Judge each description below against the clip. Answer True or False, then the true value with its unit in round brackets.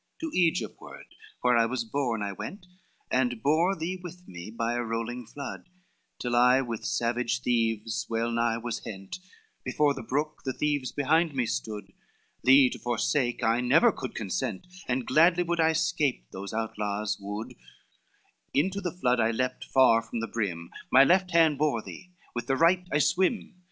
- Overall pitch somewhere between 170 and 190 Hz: False (125 Hz)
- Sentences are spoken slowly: False (175 wpm)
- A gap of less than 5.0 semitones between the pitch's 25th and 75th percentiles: False (5.3 semitones)